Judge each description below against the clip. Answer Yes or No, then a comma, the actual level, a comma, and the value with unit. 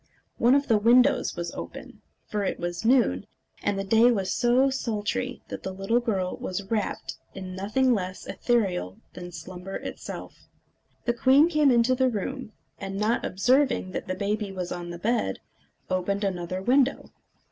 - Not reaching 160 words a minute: No, average, 165 wpm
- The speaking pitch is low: No, high, 210 Hz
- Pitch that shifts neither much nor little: Yes, average, 4.8 semitones